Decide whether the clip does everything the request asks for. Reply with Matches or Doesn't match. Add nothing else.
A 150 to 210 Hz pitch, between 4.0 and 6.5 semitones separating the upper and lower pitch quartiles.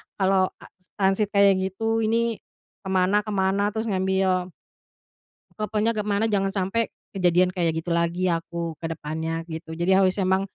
Doesn't match